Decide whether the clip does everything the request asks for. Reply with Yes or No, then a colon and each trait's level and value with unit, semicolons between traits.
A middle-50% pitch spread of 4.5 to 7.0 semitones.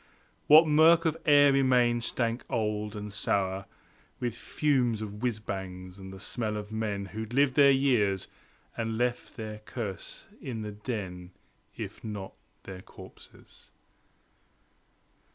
No: average, 3.9 semitones